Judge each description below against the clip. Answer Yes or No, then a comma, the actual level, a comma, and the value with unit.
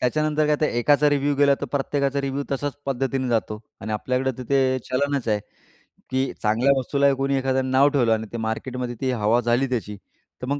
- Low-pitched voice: Yes, low, 130 Hz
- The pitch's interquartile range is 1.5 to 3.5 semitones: Yes, narrow, 2.6 semitones